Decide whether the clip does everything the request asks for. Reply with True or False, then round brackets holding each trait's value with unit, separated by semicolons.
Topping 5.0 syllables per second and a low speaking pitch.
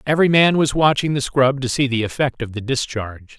True (5.8 syllables/s; 130 Hz)